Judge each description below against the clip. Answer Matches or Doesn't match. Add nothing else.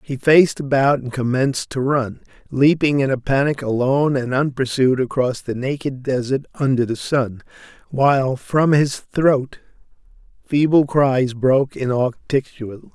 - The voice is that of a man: Matches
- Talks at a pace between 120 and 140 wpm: Matches